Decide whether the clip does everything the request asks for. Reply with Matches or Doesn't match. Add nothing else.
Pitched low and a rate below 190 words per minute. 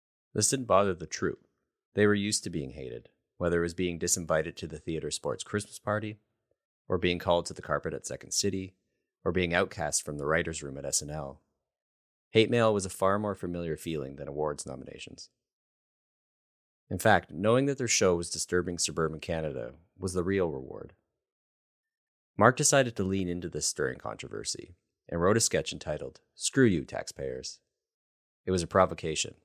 Matches